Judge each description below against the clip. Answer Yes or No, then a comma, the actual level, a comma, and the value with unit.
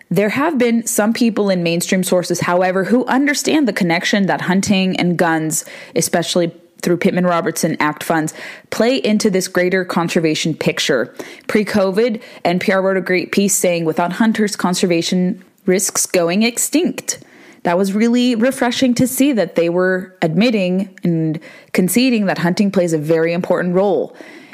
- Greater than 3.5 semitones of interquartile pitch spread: Yes, average, 4.2 semitones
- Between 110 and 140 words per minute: No, average, 150 wpm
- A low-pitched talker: No, high, 190 Hz